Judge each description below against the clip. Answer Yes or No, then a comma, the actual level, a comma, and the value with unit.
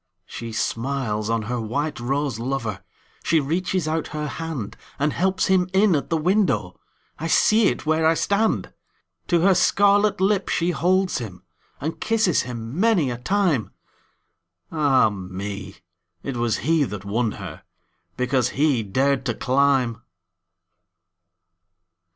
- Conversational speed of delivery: No, slow, 120 wpm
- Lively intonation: Yes, wide, 7.2 semitones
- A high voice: No, medium, 140 Hz